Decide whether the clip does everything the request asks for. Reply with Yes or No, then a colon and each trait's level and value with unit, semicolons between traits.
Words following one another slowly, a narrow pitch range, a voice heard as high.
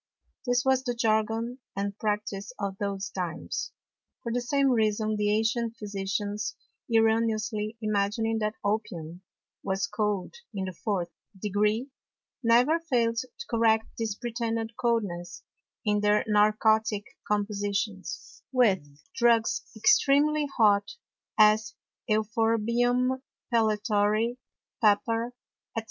Yes: slow, 105 wpm; narrow, 2.2 semitones; high, 220 Hz